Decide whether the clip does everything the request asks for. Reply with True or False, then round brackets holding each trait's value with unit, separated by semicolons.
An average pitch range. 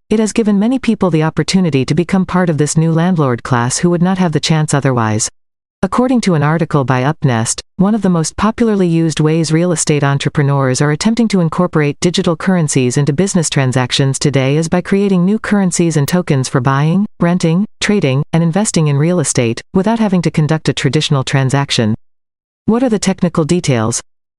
True (4.6 semitones)